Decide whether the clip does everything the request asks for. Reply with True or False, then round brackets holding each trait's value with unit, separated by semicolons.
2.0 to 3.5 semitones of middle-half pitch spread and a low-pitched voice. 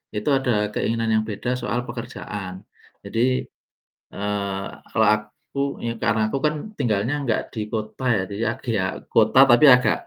True (3.1 semitones; 115 Hz)